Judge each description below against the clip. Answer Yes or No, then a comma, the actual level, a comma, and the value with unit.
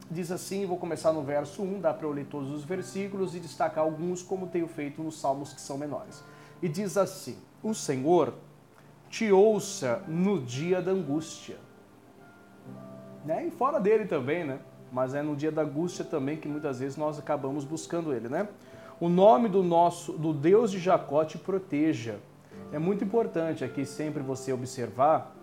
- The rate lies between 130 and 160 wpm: No, average, 170 wpm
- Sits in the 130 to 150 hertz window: No, medium, 160 Hz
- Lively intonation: No, average, 4.5 semitones